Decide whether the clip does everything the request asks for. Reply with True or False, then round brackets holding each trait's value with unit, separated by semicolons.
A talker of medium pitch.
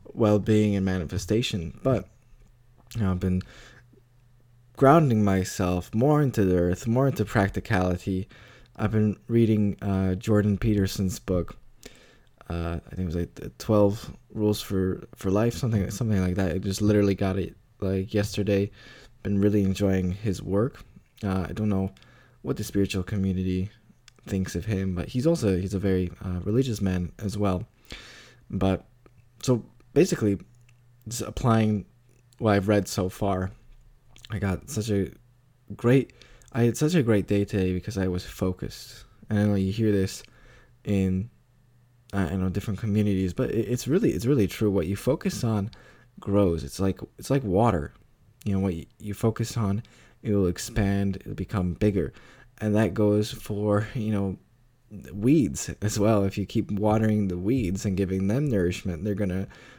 False (105 Hz)